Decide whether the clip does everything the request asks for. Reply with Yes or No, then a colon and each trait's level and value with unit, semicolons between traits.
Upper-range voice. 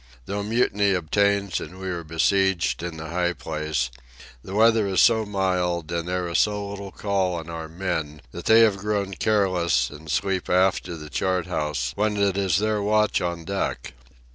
No: very low, 95 Hz